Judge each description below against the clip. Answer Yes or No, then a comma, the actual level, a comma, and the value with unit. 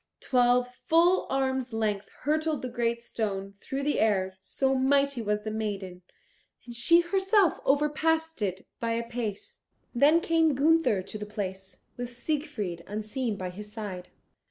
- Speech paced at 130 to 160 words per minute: Yes, average, 150 wpm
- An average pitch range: No, wide, 5.8 semitones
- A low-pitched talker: No, high, 240 Hz